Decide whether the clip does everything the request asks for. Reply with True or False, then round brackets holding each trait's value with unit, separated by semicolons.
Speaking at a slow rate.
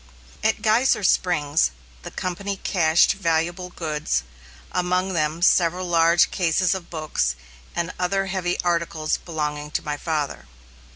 True (125 wpm)